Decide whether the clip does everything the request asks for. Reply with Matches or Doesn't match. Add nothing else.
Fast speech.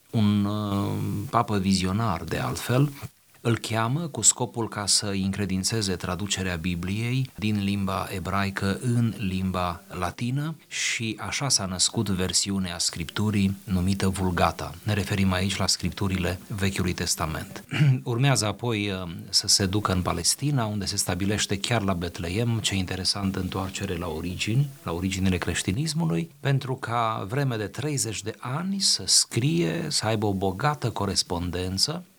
Doesn't match